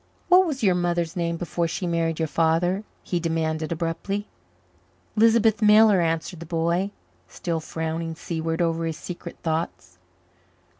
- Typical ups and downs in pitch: No, narrow, 2.1 semitones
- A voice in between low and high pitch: Yes, medium, 170 Hz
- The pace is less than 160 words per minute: Yes, average, 140 wpm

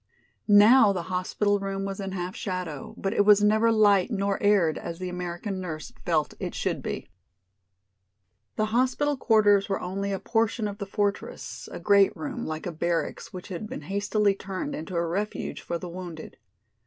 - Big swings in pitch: No, narrow, 2.6 semitones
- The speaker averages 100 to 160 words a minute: No, average, 180 wpm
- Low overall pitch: No, high, 195 Hz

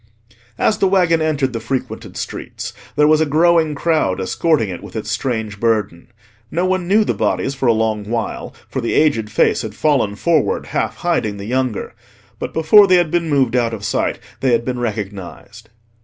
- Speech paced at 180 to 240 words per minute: Yes, average, 190 wpm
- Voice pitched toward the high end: No, low, 130 Hz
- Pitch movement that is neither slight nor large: No, wide, 6.4 semitones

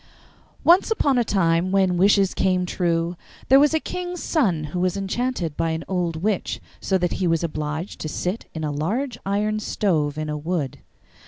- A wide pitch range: No, average, 4.4 semitones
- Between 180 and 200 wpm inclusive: Yes, average, 185 wpm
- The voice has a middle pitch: Yes, medium, 180 Hz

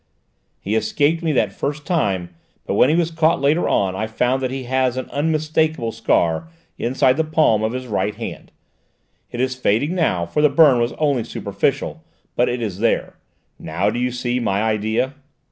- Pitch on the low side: Yes, low, 125 Hz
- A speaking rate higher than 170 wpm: Yes, average, 180 wpm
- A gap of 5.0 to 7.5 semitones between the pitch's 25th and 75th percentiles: Yes, wide, 5.5 semitones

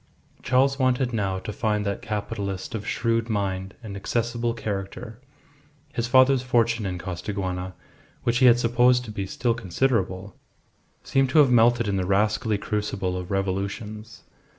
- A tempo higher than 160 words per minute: No, average, 150 wpm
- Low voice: Yes, low, 110 Hz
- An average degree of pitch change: Yes, average, 3.6 semitones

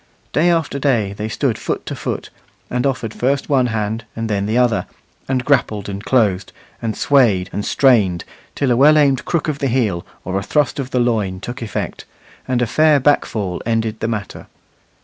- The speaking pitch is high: No, low, 120 Hz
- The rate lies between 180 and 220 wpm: Yes, average, 190 wpm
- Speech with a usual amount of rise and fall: Yes, average, 4.5 semitones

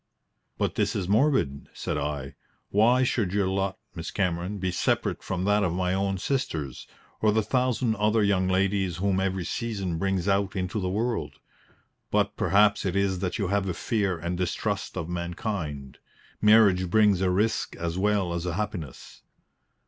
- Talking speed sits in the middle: Yes, average, 170 wpm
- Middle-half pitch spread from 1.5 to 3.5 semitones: Yes, average, 2.8 semitones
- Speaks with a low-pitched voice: Yes, very low, 95 Hz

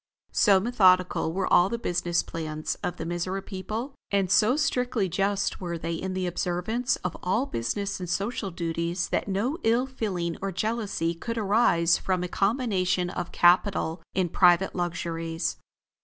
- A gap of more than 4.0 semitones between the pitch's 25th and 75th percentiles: No, average, 3.3 semitones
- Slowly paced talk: No, average, 155 wpm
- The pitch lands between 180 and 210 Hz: Yes, medium, 185 Hz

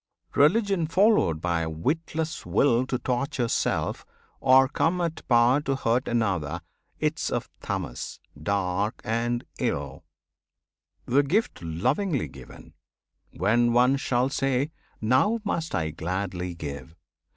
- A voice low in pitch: Yes, low, 120 Hz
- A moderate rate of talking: No, slow, 120 wpm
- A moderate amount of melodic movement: No, wide, 8.0 semitones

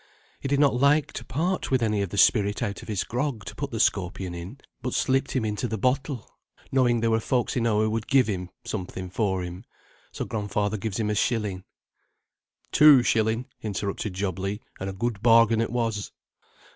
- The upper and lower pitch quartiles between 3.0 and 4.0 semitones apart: Yes, average, 3.7 semitones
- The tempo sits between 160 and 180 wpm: No, average, 195 wpm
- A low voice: Yes, low, 110 Hz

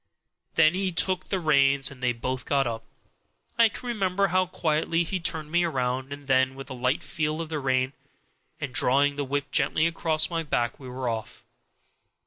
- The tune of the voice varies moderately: Yes, average, 4.2 semitones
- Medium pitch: Yes, medium, 145 Hz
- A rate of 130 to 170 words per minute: No, average, 195 wpm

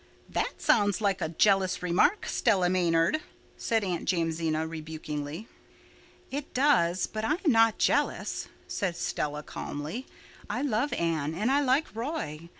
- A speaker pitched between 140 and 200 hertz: Yes, medium, 185 Hz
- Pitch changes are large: Yes, wide, 6.1 semitones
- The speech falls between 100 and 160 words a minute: Yes, average, 140 wpm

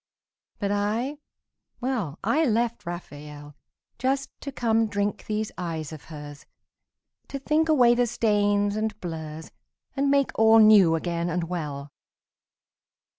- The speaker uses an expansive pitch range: Yes, wide, 6.4 semitones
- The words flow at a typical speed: No, slow, 125 wpm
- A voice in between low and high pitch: No, high, 205 Hz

